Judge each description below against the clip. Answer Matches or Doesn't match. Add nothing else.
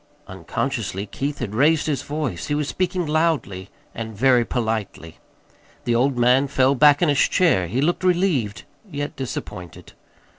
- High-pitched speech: Doesn't match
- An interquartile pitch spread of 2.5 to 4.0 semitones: Doesn't match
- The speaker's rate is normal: Matches